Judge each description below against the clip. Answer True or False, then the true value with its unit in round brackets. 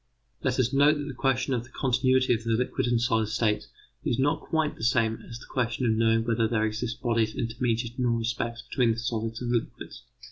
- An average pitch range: False (1.9 semitones)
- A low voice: True (120 Hz)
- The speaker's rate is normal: False (220 wpm)